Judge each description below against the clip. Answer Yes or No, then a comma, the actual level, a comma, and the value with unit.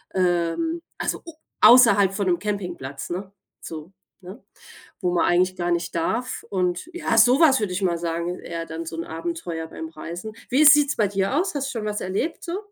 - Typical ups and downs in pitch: No, wide, 6.5 semitones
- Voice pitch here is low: No, high, 190 Hz